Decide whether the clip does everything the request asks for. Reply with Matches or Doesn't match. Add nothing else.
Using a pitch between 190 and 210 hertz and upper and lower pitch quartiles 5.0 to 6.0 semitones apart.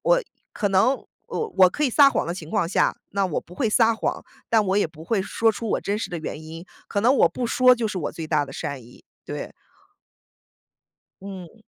Matches